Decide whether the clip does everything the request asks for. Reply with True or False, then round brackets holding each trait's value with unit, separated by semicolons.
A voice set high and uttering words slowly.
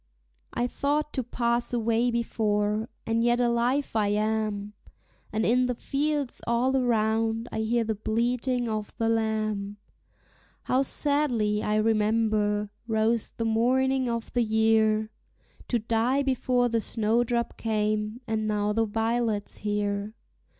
True (225 Hz; 130 wpm)